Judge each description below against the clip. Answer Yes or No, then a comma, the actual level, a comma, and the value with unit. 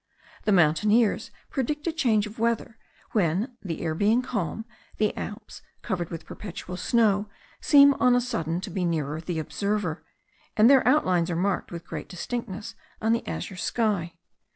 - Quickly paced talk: No, average, 160 wpm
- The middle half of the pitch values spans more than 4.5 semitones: Yes, average, 5.0 semitones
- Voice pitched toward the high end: Yes, high, 205 Hz